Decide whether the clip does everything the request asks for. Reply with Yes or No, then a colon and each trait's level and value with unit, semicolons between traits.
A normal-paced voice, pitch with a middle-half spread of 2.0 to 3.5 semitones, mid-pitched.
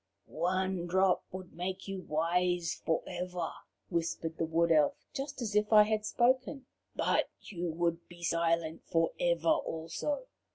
Yes: average, 150 wpm; narrow, 2.6 semitones; medium, 175 Hz